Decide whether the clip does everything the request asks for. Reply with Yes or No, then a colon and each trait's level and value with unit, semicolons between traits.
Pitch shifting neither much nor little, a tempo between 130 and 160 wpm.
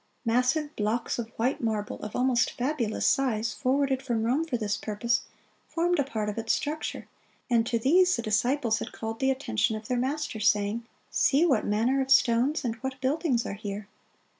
No: average, 3.5 semitones; average, 185 wpm